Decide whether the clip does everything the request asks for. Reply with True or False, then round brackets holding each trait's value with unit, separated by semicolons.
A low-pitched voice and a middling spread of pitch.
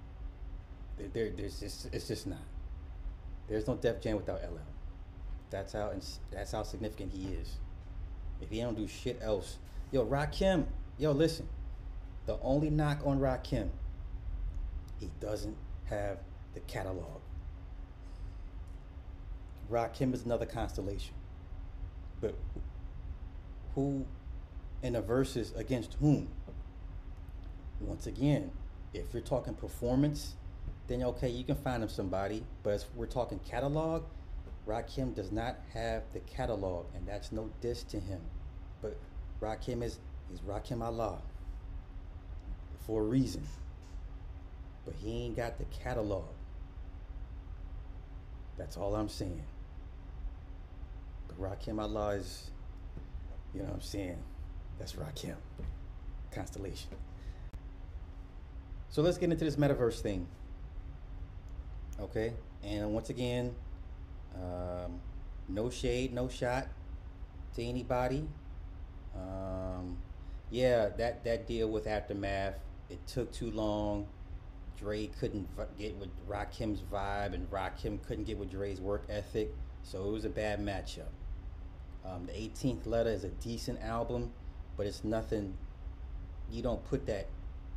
False (95 Hz; 6.2 semitones)